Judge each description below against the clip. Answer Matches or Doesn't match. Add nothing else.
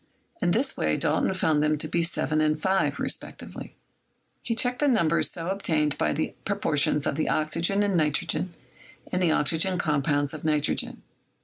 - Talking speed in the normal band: Matches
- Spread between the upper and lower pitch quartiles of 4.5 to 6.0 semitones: Doesn't match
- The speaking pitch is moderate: Matches